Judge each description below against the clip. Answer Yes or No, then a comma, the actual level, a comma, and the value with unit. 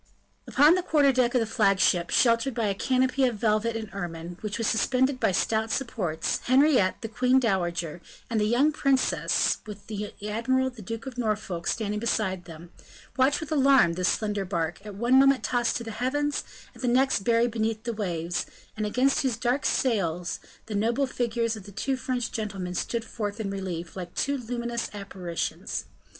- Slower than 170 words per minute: No, average, 185 wpm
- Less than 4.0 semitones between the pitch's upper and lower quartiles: No, average, 4.4 semitones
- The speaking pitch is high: Yes, high, 225 Hz